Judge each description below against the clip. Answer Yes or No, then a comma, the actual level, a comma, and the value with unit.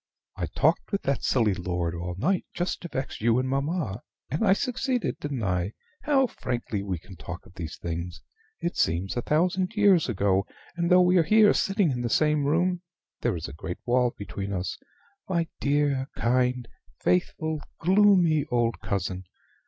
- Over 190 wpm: No, average, 175 wpm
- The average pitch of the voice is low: Yes, low, 130 Hz